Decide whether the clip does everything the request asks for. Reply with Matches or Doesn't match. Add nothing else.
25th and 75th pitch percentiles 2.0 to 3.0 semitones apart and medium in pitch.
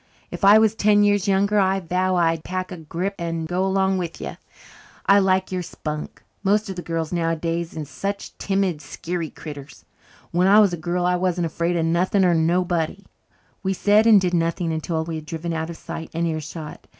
Matches